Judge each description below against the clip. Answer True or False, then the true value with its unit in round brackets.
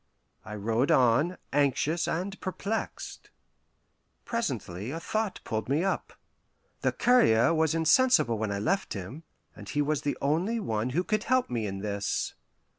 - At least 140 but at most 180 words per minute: True (150 wpm)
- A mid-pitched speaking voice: True (145 Hz)